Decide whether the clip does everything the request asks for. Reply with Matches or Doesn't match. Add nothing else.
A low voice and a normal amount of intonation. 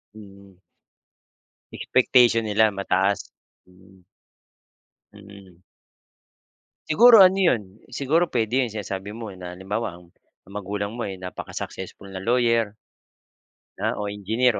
Matches